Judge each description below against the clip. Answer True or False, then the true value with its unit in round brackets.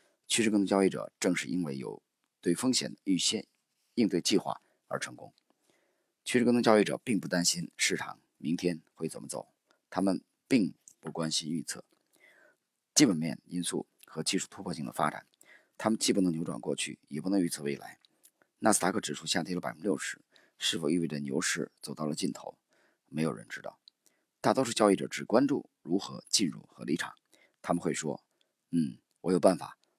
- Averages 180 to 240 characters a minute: False (275 characters per minute)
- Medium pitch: False (90 Hz)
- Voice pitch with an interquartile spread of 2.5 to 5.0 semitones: True (4.5 semitones)